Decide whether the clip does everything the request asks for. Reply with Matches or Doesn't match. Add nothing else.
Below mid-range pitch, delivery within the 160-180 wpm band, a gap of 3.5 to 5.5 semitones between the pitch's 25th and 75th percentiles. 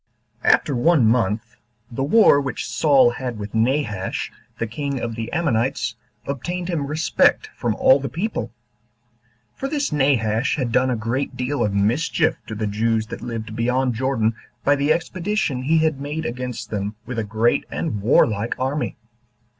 Matches